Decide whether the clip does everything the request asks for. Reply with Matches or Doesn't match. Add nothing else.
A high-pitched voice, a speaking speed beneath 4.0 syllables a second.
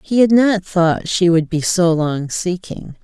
Doesn't match